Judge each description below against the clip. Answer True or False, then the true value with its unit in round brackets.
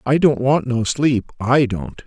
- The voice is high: False (130 Hz)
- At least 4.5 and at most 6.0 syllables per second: False (3.9 syllables/s)